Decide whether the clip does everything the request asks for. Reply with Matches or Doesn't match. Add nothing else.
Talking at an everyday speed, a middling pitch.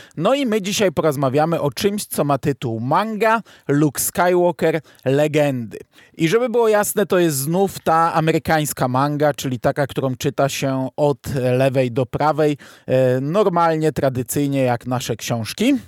Matches